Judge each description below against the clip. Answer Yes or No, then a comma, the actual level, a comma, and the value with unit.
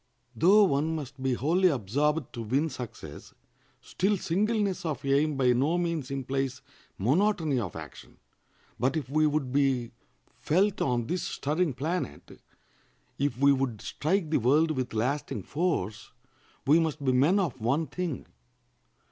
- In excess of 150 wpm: No, average, 145 wpm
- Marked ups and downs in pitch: No, average, 4.4 semitones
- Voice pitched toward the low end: No, medium, 145 Hz